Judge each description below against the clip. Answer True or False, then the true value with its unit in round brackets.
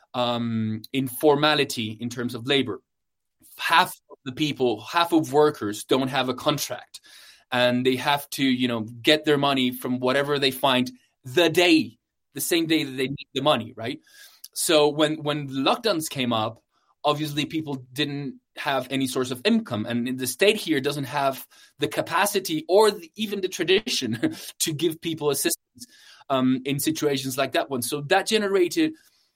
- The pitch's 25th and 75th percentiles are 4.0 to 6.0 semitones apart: True (4.3 semitones)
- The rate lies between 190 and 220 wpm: False (165 wpm)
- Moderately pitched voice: True (145 Hz)